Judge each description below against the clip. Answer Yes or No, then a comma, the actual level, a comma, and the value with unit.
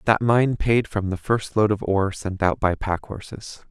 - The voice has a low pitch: Yes, low, 105 Hz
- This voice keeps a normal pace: No, fast, 225 wpm